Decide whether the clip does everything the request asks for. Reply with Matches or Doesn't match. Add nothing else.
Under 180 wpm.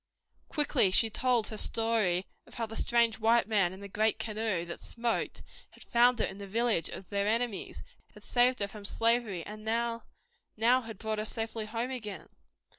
Doesn't match